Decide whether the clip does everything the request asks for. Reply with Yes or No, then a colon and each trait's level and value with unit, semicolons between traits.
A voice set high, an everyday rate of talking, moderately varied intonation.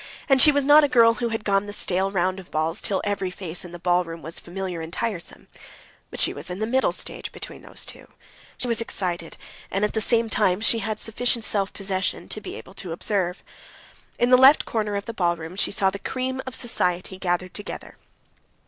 No: high, 200 Hz; fast, 215 wpm; average, 4.2 semitones